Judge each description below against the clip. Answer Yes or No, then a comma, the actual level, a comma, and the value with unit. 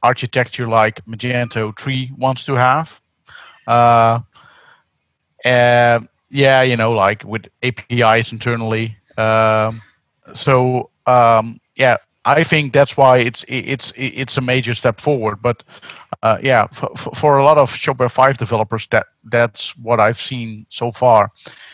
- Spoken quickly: No, slow, 135 wpm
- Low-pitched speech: Yes, low, 120 Hz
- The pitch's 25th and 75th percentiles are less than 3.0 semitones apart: Yes, narrow, 2.4 semitones